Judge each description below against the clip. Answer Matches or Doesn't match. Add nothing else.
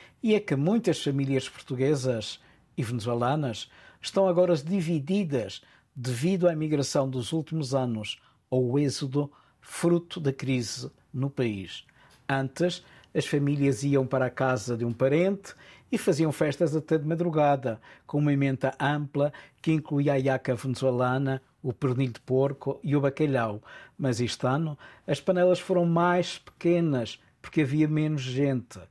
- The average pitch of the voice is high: Doesn't match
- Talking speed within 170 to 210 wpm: Doesn't match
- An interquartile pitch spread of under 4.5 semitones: Matches